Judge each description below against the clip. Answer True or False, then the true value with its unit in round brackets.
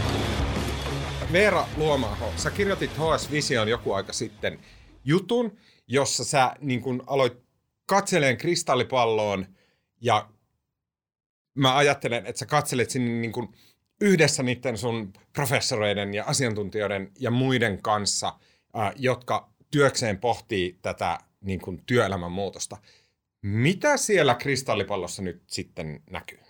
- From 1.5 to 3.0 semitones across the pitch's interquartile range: False (5.5 semitones)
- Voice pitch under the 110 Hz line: False (125 Hz)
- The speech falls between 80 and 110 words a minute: True (105 wpm)